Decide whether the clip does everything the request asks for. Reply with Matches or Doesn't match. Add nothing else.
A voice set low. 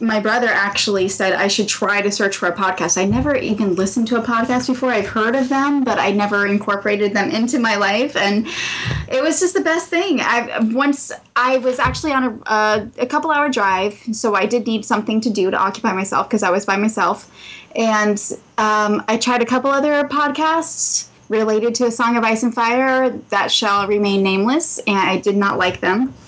Doesn't match